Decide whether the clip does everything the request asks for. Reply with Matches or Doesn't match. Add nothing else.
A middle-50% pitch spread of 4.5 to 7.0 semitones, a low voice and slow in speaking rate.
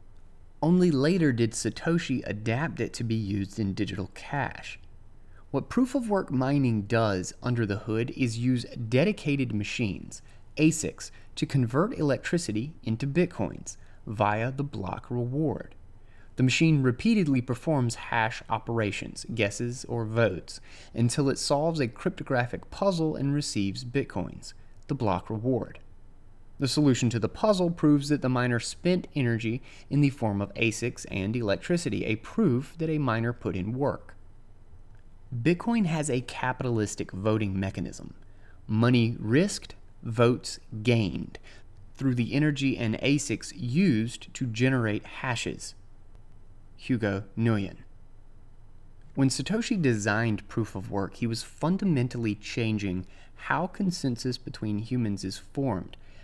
Matches